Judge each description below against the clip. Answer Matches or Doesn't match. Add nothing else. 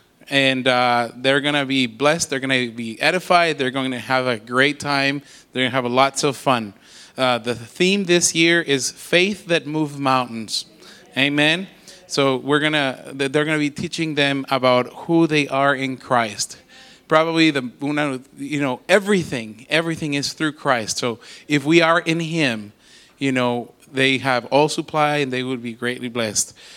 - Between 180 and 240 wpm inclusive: Doesn't match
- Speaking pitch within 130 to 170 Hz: Matches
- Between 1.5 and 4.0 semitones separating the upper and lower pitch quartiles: Matches